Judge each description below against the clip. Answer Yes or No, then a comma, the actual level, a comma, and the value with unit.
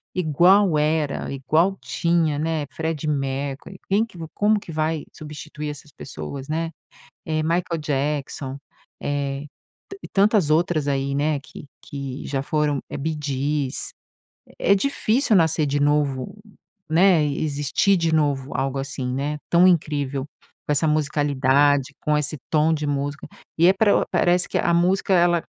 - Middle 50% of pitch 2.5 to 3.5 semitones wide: Yes, average, 3.1 semitones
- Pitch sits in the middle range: Yes, medium, 150 Hz